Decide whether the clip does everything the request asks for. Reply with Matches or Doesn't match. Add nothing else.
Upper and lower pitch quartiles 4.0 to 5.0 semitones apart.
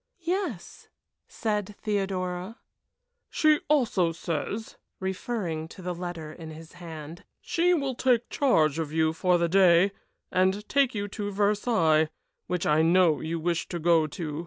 Matches